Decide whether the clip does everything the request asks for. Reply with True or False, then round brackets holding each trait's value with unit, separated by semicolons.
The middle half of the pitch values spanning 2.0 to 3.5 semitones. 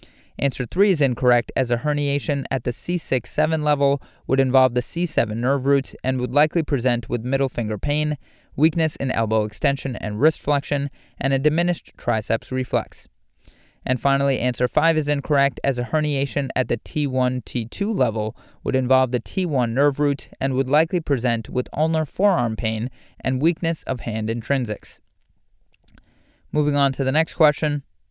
True (3.0 semitones)